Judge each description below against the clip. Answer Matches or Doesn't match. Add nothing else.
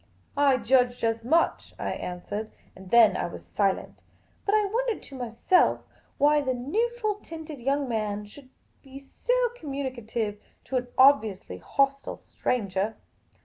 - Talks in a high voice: Matches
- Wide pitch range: Doesn't match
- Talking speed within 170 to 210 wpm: Doesn't match